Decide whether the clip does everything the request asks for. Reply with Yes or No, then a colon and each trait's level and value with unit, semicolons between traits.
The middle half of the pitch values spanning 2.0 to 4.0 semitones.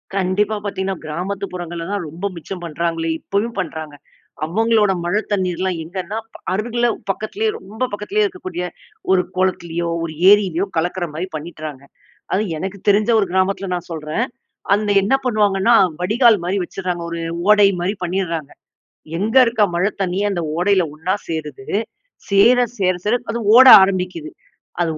Yes: average, 3.4 semitones